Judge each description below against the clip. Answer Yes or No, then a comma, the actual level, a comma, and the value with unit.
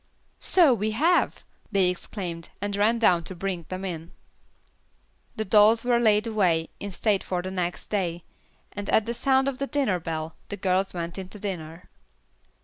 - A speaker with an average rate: Yes, average, 170 wpm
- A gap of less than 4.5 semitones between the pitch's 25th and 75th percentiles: Yes, average, 3.7 semitones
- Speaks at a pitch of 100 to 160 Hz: No, high, 195 Hz